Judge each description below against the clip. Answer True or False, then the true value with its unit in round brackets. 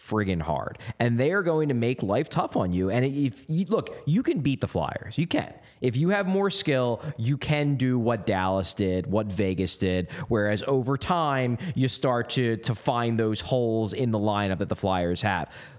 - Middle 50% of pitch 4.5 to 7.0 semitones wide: True (5.2 semitones)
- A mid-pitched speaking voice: False (120 Hz)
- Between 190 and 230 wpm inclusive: True (200 wpm)